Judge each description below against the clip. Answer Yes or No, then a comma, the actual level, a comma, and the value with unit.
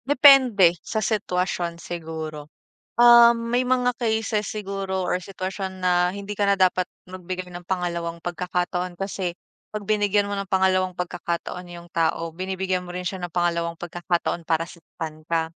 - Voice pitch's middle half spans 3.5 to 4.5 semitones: No, narrow, 2.6 semitones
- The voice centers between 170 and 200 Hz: Yes, medium, 185 Hz